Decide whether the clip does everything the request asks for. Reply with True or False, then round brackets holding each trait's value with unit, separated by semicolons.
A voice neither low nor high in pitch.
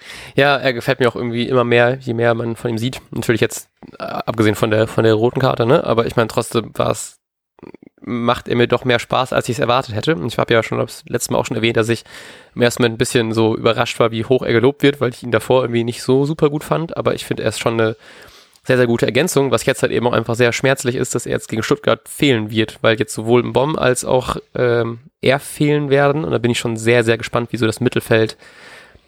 False (120 Hz)